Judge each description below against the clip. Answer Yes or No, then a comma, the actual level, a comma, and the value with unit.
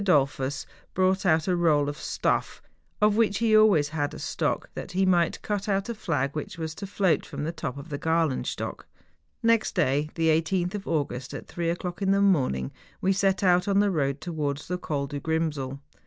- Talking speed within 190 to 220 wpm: Yes, average, 200 wpm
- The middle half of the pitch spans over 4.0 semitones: Yes, average, 4.9 semitones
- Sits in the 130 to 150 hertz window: No, medium, 165 Hz